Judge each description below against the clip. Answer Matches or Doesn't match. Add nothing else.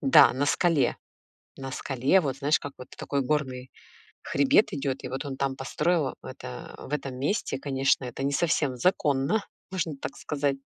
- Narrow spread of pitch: Matches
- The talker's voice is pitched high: Doesn't match